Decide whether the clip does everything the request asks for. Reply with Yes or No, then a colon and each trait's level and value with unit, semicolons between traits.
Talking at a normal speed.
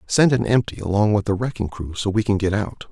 No: fast, 265 wpm